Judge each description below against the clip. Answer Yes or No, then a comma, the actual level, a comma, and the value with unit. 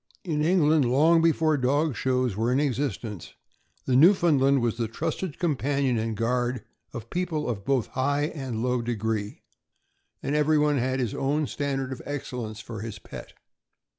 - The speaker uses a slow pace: No, average, 165 wpm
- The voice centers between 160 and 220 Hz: No, low, 135 Hz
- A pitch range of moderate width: Yes, average, 3.9 semitones